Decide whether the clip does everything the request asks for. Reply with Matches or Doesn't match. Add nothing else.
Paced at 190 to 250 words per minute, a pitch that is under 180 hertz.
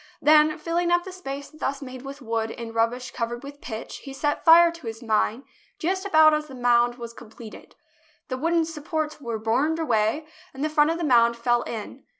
Doesn't match